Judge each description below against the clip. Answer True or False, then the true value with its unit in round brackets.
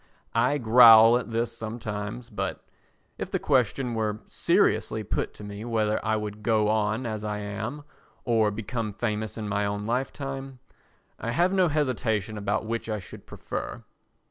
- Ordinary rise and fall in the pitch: False (2.3 semitones)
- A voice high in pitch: False (110 Hz)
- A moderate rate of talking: True (160 wpm)